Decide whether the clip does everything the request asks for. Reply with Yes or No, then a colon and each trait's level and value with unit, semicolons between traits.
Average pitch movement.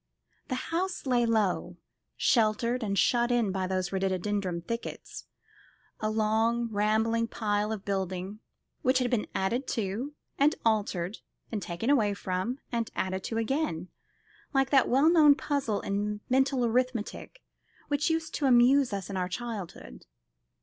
Yes: average, 4.4 semitones